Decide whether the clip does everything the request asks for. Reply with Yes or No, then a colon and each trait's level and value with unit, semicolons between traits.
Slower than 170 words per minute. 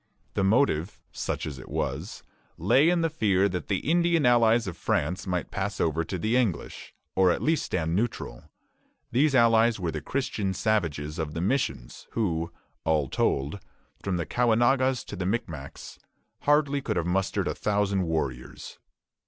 Yes: average, 160 wpm